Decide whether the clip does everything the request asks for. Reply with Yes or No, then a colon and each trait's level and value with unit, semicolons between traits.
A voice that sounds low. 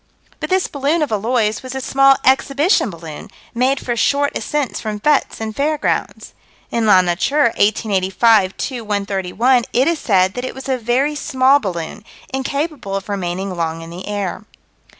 No: high, 235 Hz